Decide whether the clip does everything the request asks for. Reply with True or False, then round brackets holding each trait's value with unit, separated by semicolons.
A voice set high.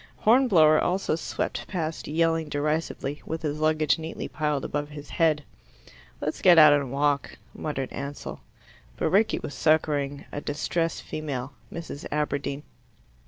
False (150 Hz)